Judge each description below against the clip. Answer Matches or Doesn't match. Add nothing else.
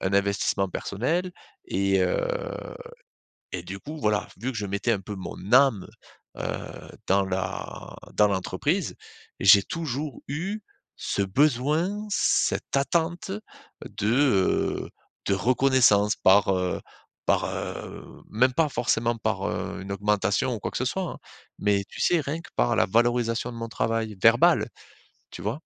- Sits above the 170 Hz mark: Doesn't match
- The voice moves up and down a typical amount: Doesn't match